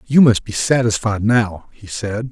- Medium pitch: No, low, 110 Hz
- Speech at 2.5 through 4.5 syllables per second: Yes, 4.1 syllables/s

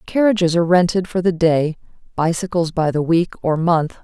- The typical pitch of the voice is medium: Yes, medium, 170 Hz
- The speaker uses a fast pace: No, average, 180 wpm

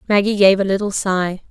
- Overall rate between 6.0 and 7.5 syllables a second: No, 5.4 syllables/s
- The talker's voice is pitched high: Yes, high, 195 Hz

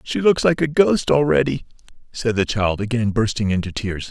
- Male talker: Yes, male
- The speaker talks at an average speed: Yes, average, 190 wpm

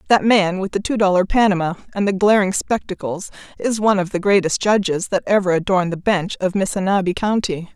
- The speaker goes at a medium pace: Yes, average, 195 wpm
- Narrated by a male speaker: No, female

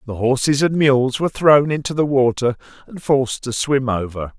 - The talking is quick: No, average, 190 wpm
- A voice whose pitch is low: Yes, low, 130 Hz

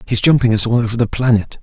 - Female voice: No, male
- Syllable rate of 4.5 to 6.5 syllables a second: No, 6.7 syllables/s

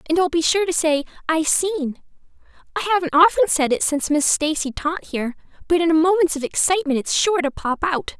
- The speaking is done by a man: No, female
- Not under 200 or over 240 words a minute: Yes, fast, 205 wpm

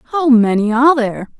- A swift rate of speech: No, average, 170 wpm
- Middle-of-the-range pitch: No, very high, 250 Hz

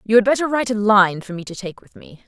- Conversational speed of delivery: No, fast, 315 wpm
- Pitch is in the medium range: No, high, 210 Hz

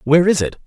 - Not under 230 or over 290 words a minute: Yes, fast, 270 wpm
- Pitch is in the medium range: Yes, medium, 155 Hz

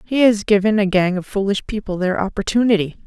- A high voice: Yes, high, 200 Hz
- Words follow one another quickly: No, average, 195 wpm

